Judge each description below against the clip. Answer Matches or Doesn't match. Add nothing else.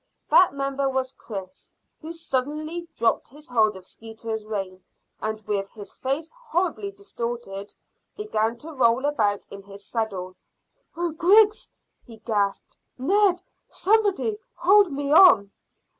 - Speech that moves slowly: Matches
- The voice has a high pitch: Matches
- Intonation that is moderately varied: Doesn't match